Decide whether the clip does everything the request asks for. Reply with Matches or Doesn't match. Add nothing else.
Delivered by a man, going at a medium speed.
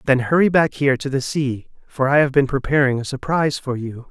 Doesn't match